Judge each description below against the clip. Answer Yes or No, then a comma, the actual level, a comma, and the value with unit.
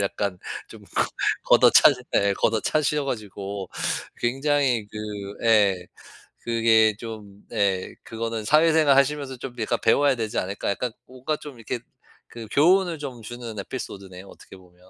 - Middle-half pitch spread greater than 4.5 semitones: Yes, average, 5.3 semitones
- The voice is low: Yes, low, 115 Hz